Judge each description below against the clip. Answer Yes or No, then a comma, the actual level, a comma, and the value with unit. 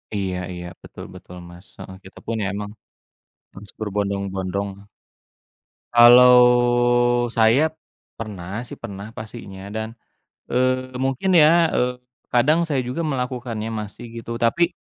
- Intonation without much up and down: No, average, 4.1 semitones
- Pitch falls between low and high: No, low, 115 Hz